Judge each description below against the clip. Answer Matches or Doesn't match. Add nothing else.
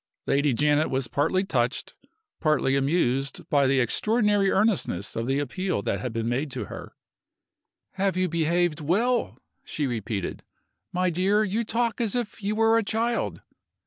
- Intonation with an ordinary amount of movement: Doesn't match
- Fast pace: Doesn't match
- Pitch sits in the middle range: Matches